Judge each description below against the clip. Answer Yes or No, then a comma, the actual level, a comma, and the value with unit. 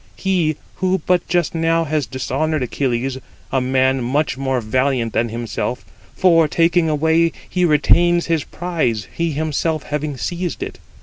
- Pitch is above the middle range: No, medium, 155 Hz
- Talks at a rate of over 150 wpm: No, average, 145 wpm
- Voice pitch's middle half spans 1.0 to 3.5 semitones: No, average, 4.2 semitones